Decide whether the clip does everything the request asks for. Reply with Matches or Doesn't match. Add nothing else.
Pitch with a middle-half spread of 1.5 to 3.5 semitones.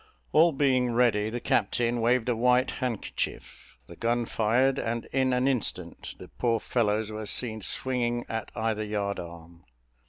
Matches